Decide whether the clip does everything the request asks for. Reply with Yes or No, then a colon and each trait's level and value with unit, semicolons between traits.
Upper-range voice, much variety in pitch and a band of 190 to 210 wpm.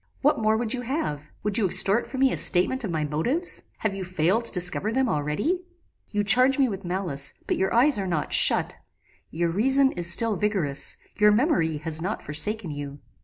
Yes: high, 200 Hz; wide, 6.5 semitones; average, 200 wpm